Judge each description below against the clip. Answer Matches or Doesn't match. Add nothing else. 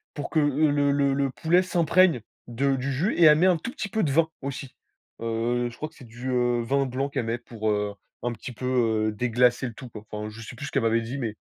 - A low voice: Matches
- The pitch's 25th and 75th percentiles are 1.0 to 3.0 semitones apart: Doesn't match